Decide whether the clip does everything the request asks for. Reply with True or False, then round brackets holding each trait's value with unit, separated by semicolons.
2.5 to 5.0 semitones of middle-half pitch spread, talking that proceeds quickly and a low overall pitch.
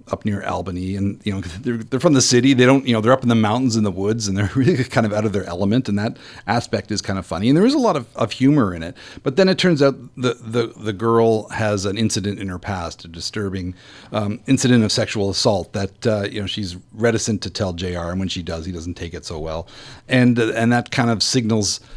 True (4.0 semitones; 265 wpm; 110 Hz)